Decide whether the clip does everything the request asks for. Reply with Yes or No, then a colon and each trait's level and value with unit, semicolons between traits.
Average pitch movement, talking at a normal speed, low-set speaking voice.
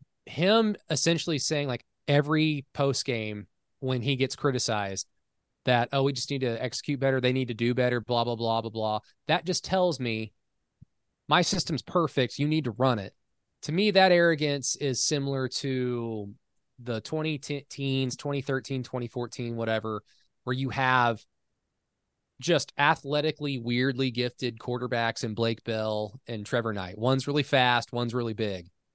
Yes: average, 3.6 semitones; average, 150 wpm; low, 130 Hz